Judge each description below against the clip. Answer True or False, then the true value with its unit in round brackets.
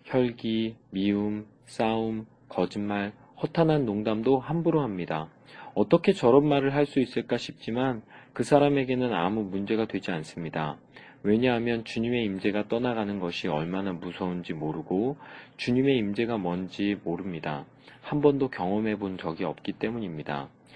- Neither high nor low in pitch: False (110 Hz)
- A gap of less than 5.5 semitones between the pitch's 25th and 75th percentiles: True (5.1 semitones)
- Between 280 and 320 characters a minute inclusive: True (310 characters per minute)